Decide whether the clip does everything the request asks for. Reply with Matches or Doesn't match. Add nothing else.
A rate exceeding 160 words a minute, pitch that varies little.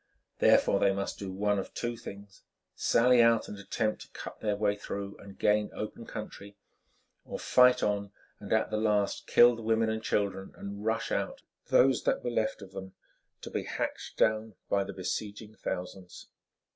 Matches